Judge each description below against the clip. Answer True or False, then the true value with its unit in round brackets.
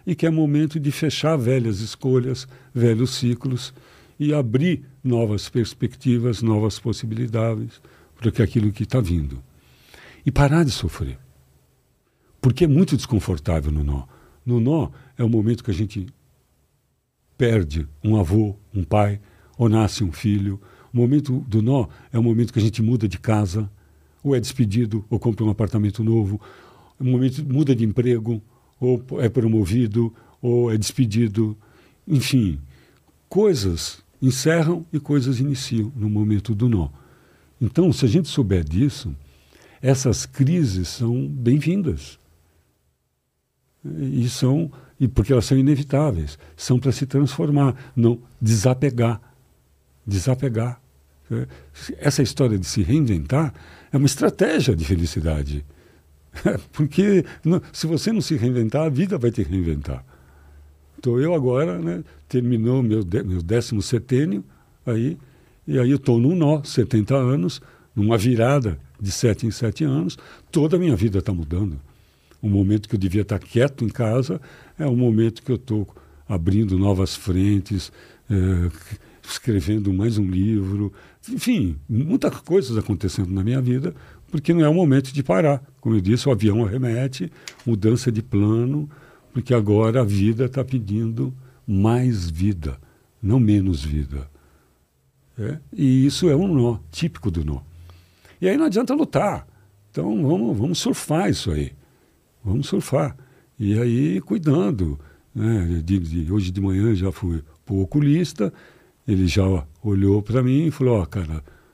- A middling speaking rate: True (145 wpm)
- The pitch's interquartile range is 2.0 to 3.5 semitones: False (5.4 semitones)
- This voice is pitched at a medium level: False (115 Hz)